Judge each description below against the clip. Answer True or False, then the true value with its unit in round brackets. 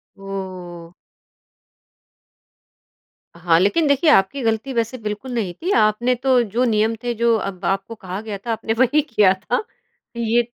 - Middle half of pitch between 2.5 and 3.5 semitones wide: False (4.0 semitones)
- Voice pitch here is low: False (220 Hz)